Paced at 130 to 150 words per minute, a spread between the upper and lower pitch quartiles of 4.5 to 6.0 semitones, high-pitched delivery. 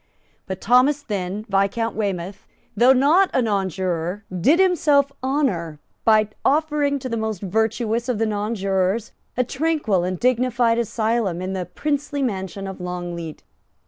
Yes: average, 140 wpm; wide, 5.4 semitones; high, 220 Hz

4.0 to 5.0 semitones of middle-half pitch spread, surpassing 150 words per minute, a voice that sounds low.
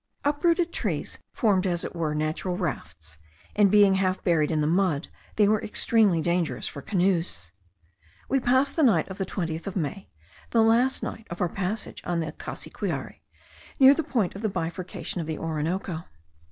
No: average, 4.7 semitones; average, 170 wpm; medium, 185 Hz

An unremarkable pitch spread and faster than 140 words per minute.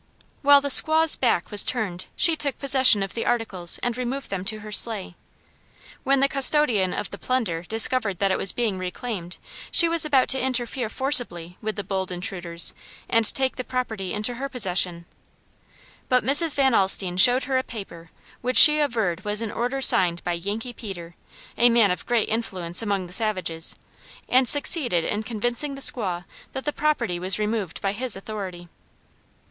No: wide, 5.7 semitones; average, 175 wpm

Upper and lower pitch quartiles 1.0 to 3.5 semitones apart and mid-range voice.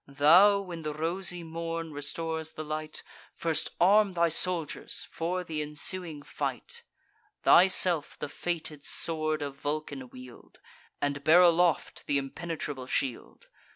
Yes: average, 2.9 semitones; medium, 160 Hz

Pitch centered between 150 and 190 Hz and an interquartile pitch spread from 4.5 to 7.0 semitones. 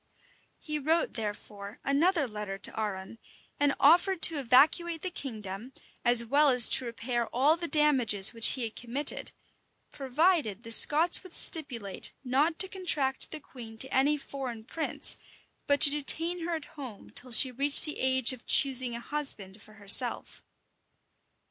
No: very high, 265 Hz; average, 4.8 semitones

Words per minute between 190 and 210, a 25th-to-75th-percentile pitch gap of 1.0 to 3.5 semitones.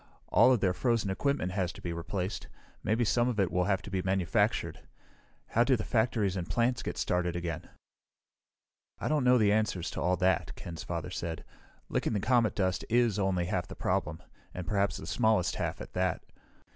No: average, 195 wpm; average, 4.2 semitones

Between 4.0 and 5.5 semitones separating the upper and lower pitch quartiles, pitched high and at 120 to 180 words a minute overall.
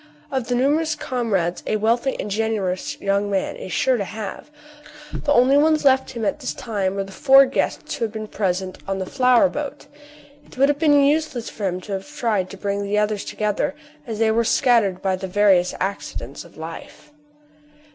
No: average, 5.1 semitones; high, 220 Hz; average, 195 wpm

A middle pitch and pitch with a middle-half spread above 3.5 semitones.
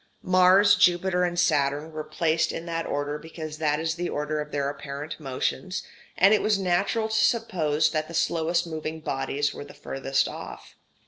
No: medium, 160 Hz; average, 3.1 semitones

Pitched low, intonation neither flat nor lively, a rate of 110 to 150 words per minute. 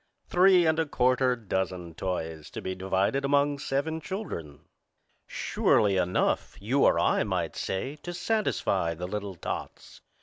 No: low, 115 Hz; wide, 7.8 semitones; average, 140 wpm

